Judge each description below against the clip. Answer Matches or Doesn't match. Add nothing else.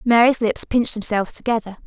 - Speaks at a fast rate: Doesn't match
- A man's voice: Doesn't match